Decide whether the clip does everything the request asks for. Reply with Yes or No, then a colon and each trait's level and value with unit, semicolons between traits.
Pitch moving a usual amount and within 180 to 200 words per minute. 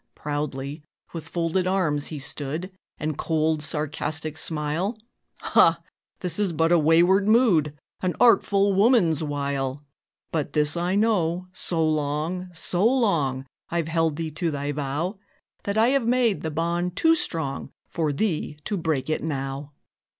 No: average, 3.8 semitones; average, 145 wpm